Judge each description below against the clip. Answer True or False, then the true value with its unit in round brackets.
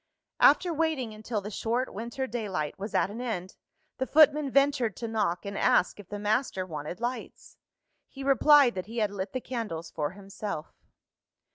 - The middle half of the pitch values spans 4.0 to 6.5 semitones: True (5.0 semitones)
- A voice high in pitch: True (220 Hz)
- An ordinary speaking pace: True (170 wpm)